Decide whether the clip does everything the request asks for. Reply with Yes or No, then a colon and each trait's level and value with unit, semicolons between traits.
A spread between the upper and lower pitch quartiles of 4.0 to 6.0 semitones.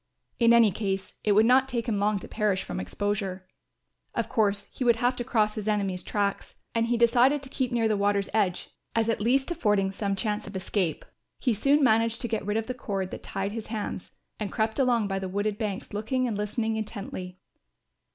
No: average, 2.8 semitones